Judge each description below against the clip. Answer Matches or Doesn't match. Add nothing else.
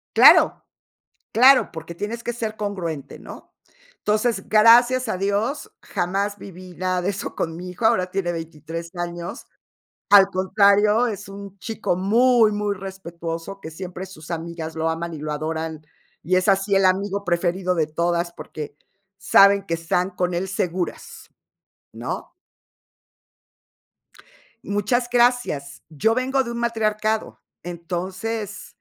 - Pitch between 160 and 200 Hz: Matches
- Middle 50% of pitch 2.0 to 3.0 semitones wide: Doesn't match